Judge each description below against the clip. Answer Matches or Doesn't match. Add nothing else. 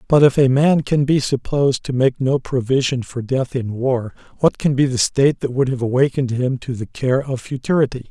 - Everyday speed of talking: Doesn't match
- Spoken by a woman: Doesn't match